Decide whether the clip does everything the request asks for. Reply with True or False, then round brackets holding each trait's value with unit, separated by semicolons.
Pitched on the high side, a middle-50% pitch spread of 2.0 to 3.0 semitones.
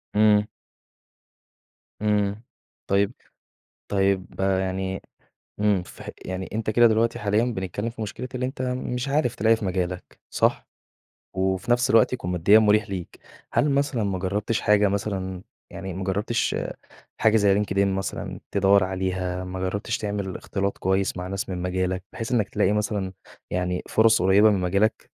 False (100 Hz; 2.7 semitones)